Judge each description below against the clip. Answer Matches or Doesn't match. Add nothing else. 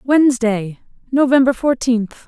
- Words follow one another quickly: Doesn't match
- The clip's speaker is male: Doesn't match